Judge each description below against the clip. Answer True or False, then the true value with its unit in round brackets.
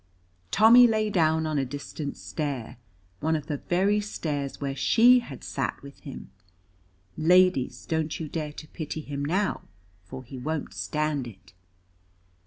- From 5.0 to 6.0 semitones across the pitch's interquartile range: False (4.3 semitones)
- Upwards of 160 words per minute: False (150 wpm)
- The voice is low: False (155 Hz)